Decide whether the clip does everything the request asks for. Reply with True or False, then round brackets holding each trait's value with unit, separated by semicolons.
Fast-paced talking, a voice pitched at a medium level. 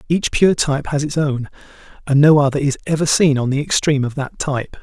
True (225 wpm; 145 Hz)